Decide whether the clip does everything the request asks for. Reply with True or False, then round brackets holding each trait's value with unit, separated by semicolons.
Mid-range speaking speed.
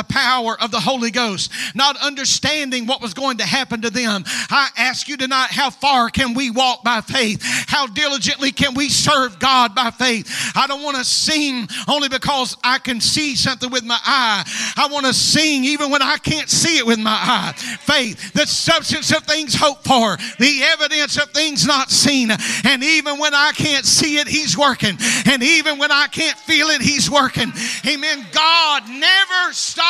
True (195 wpm)